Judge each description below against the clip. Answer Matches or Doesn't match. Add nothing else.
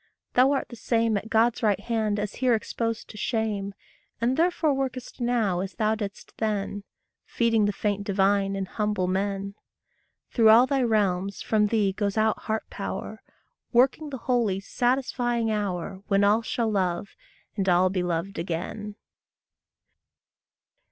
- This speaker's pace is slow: Doesn't match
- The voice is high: Matches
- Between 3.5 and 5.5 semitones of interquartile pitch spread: Doesn't match